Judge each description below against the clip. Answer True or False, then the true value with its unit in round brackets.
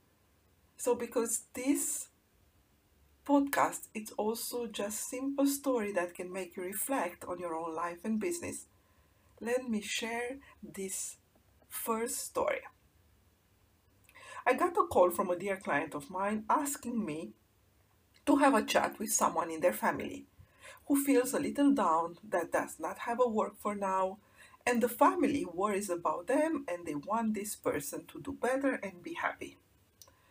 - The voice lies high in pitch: True (205 Hz)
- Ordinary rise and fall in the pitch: False (7.5 semitones)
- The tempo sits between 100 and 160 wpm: True (150 wpm)